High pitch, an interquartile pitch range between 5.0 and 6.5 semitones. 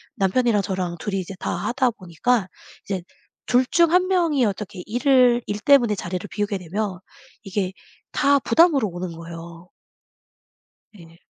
Yes: high, 205 Hz; wide, 5.6 semitones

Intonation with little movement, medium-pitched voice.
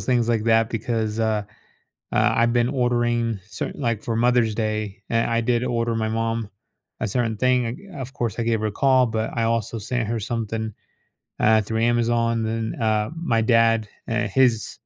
No: narrow, 1.3 semitones; low, 115 Hz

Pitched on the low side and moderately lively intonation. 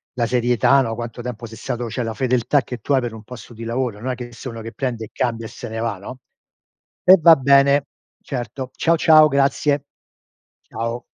Yes: low, 125 Hz; average, 3.1 semitones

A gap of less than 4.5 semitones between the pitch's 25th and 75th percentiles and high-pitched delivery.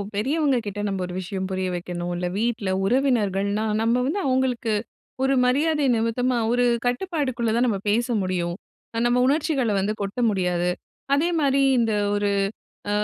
No: average, 5.1 semitones; high, 230 Hz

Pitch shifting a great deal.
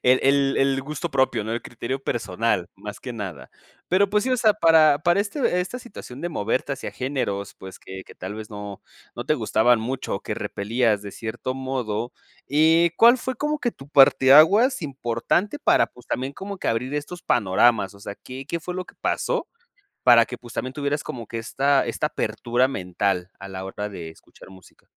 Yes: wide, 6.3 semitones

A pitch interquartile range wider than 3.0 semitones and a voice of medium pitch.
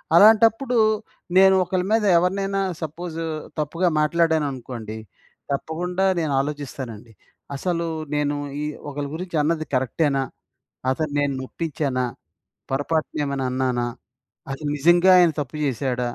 Yes: average, 4.3 semitones; medium, 150 Hz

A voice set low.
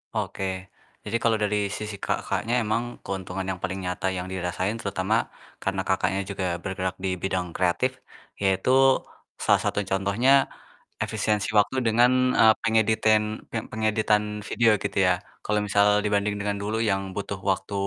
Yes: low, 100 Hz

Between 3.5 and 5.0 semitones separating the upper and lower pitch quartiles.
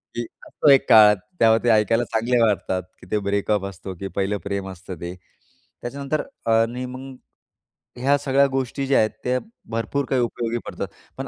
Yes: average, 4.2 semitones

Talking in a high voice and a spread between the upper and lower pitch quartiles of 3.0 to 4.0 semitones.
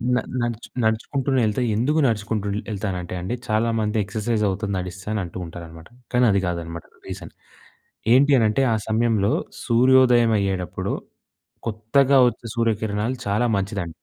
No: low, 110 Hz; average, 3.4 semitones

